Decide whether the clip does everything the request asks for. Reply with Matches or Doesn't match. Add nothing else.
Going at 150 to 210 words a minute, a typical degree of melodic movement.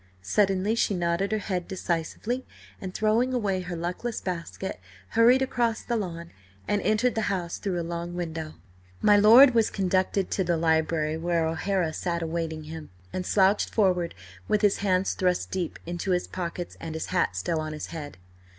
Matches